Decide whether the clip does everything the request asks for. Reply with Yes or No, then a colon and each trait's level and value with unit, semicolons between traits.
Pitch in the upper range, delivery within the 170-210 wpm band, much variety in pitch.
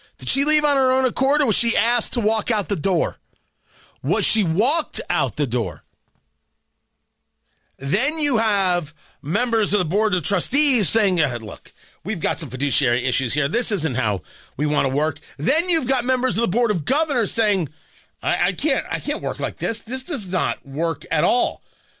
Yes: high, 205 Hz; average, 195 wpm; wide, 8.2 semitones